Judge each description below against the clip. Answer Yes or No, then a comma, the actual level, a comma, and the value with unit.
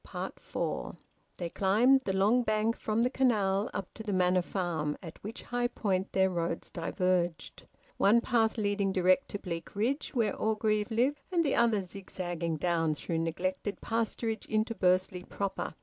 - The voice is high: Yes, high, 200 Hz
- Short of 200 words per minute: Yes, average, 155 wpm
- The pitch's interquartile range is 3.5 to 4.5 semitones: Yes, average, 3.8 semitones